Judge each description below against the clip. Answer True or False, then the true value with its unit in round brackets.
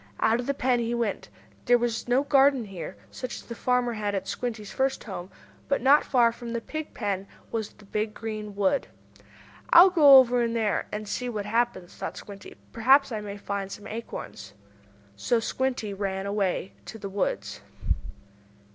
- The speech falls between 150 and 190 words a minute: True (180 wpm)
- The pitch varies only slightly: False (3.7 semitones)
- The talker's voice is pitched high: True (225 Hz)